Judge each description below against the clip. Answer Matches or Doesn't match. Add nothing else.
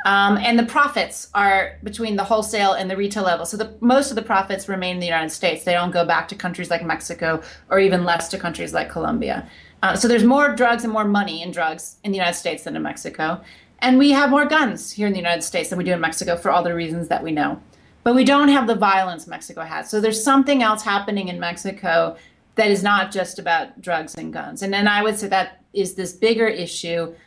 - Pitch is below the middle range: Doesn't match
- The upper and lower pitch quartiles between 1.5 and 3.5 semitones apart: Doesn't match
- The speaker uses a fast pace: Matches